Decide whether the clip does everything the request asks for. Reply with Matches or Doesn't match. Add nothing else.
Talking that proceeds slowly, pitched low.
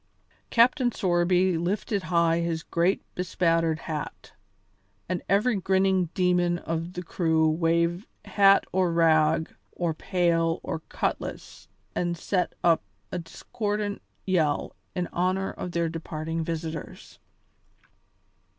Doesn't match